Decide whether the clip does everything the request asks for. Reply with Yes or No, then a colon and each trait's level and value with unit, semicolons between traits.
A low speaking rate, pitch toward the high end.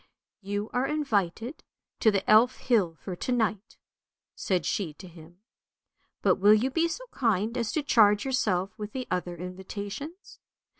No: average, 165 wpm; high, 210 Hz